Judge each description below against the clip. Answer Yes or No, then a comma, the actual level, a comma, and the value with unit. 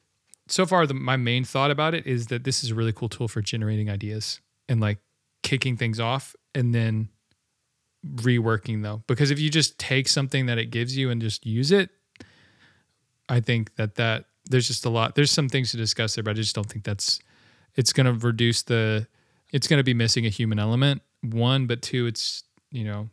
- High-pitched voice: No, low, 120 Hz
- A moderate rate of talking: No, fast, 210 wpm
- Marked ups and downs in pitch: No, average, 3.1 semitones